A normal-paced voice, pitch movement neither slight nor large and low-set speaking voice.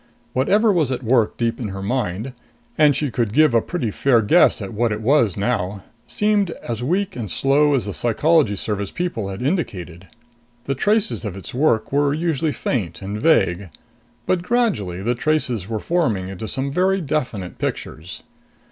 No: average, 175 wpm; wide, 7.2 semitones; low, 120 Hz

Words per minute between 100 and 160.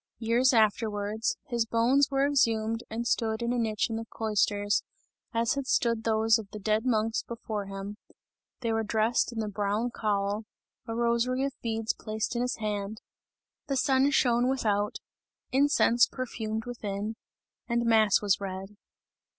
Yes: average, 155 wpm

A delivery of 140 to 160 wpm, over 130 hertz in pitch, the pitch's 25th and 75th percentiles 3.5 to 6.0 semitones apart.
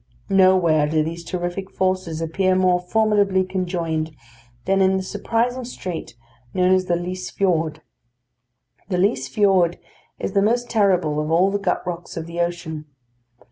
No: average, 150 wpm; medium, 185 Hz; narrow, 2.5 semitones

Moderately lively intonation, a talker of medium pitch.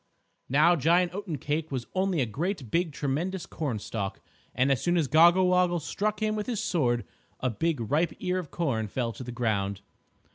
No: wide, 6.2 semitones; medium, 155 Hz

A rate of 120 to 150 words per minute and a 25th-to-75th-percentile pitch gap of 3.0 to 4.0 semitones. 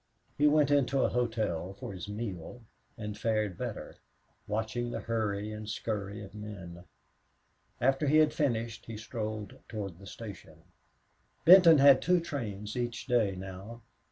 Yes: average, 145 wpm; average, 3.5 semitones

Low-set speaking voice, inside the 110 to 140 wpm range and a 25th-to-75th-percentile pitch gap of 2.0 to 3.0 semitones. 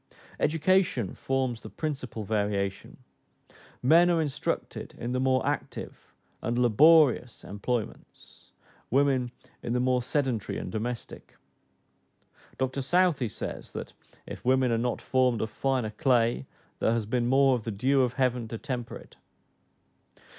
Yes: low, 125 Hz; slow, 135 wpm; narrow, 2.6 semitones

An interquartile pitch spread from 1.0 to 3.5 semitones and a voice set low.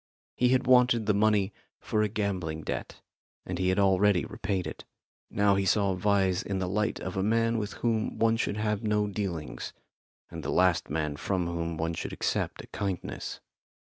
Yes: narrow, 2.6 semitones; low, 100 Hz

